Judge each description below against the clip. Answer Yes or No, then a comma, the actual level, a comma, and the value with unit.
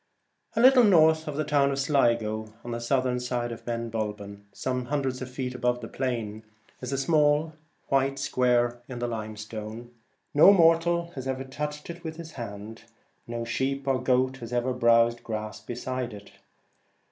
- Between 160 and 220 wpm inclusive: Yes, average, 170 wpm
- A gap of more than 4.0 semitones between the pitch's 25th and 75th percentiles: No, average, 3.1 semitones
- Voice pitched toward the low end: Yes, low, 125 Hz